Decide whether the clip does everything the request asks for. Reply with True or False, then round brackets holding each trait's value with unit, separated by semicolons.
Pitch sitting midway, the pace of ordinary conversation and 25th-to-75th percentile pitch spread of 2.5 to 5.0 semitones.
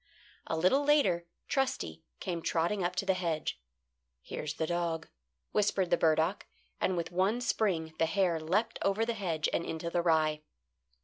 True (175 Hz; 165 wpm; 3.5 semitones)